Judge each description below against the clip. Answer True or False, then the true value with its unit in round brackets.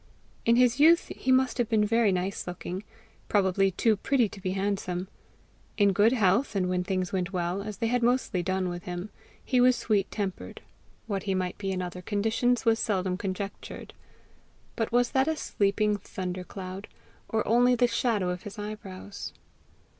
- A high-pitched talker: True (200 Hz)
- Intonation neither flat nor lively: True (3.8 semitones)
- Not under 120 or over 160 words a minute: False (175 wpm)